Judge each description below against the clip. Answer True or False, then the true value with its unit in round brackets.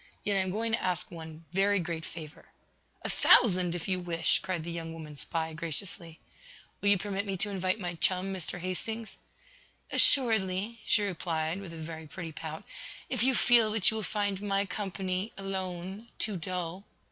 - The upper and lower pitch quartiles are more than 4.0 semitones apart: False (3.3 semitones)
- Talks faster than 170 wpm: True (180 wpm)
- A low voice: False (185 Hz)